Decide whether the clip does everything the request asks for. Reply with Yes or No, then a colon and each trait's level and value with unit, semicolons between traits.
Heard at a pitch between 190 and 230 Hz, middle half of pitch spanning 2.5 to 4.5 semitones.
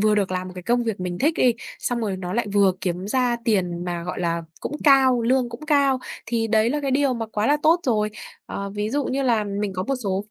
No: high, 220 Hz; average, 5.2 semitones